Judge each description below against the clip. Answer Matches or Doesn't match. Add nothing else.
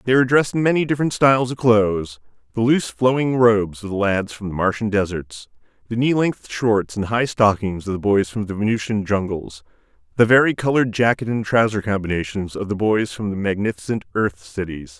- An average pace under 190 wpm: Doesn't match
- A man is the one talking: Matches